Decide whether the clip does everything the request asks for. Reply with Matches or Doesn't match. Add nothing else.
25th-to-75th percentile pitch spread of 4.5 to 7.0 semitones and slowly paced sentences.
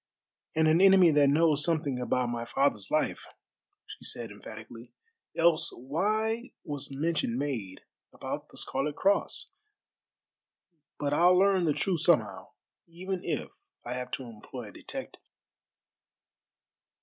Matches